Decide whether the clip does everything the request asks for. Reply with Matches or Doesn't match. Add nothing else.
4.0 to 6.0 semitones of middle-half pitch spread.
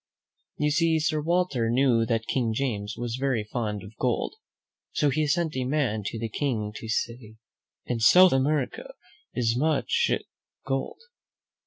Matches